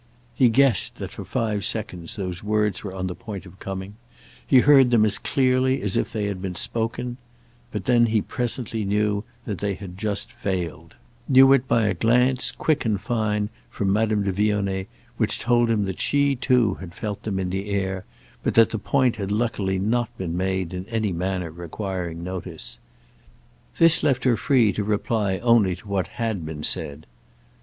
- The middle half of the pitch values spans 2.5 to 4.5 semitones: Yes, average, 3.7 semitones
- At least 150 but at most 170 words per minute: No, average, 180 wpm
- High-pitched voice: No, low, 105 Hz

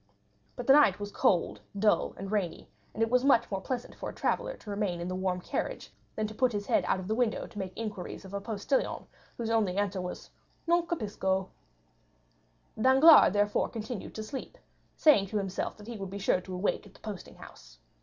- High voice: Yes, high, 205 Hz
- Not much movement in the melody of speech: No, average, 3.5 semitones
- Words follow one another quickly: Yes, fast, 215 wpm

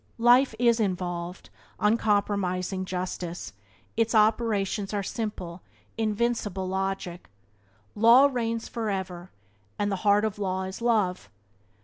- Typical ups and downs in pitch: Yes, average, 3.4 semitones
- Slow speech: Yes, slow, 105 wpm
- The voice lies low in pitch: No, high, 205 Hz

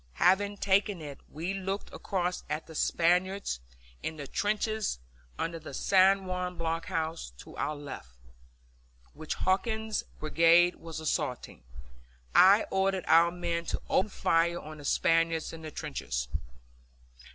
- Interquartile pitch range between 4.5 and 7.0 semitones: No, average, 3.3 semitones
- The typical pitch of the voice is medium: Yes, medium, 170 Hz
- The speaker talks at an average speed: No, slow, 130 wpm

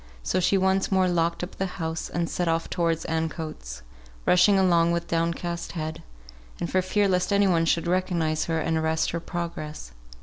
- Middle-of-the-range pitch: Yes, medium, 170 Hz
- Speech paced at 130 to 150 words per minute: No, average, 180 wpm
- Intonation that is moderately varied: No, narrow, 2.0 semitones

